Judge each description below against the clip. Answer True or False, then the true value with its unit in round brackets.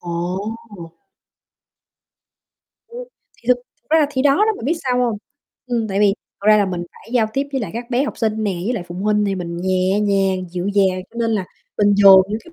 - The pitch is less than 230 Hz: True (210 Hz)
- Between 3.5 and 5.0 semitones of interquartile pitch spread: True (4.2 semitones)